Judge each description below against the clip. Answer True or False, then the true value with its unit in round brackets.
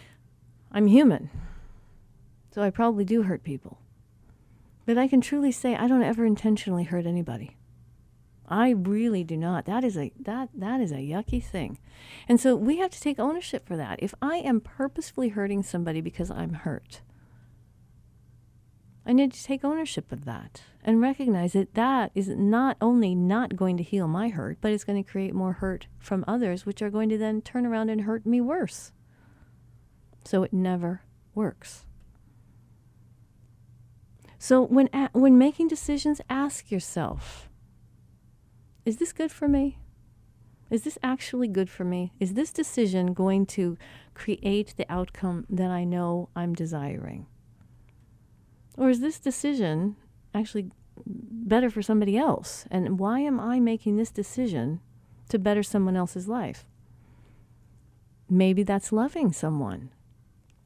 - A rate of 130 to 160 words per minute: True (150 wpm)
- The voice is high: True (195 Hz)